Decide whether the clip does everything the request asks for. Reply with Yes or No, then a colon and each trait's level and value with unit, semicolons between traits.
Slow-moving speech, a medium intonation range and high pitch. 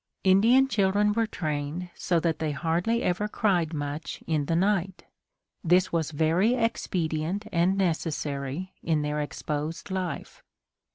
No: slow, 130 wpm; average, 3.8 semitones; medium, 170 Hz